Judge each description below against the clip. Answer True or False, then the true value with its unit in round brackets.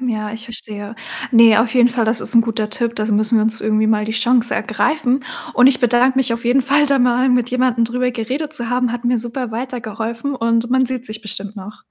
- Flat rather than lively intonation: True (2.2 semitones)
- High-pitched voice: True (235 Hz)